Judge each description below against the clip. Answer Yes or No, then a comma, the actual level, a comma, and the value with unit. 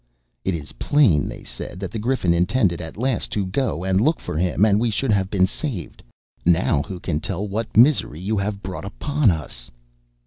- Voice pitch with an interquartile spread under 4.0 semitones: No, average, 4.3 semitones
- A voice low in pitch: Yes, low, 100 Hz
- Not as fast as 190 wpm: No, average, 200 wpm